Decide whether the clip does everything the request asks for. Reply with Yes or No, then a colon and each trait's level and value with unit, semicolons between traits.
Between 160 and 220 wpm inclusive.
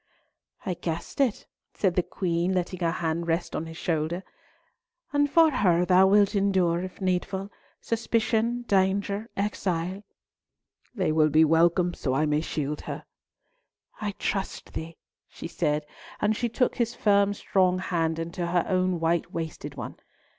No: average, 150 wpm